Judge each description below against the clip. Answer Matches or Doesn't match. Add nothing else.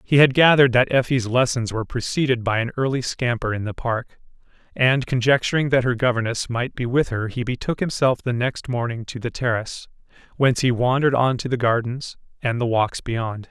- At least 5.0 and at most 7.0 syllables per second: Matches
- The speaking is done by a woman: Doesn't match